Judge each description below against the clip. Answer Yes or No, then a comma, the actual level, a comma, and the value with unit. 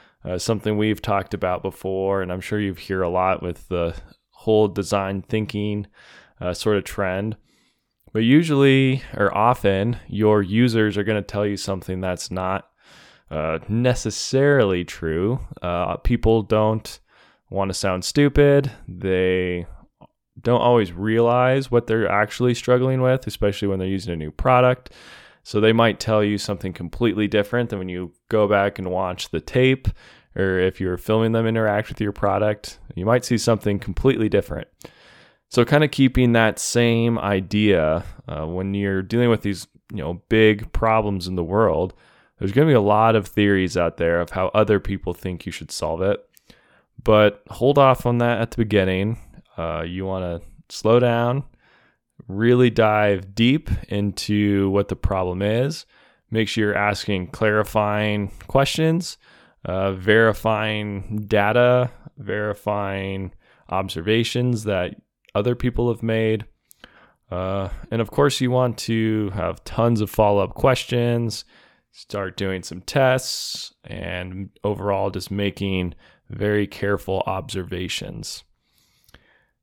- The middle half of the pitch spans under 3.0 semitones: No, average, 3.3 semitones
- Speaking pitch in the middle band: No, low, 105 Hz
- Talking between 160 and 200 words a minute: No, average, 150 wpm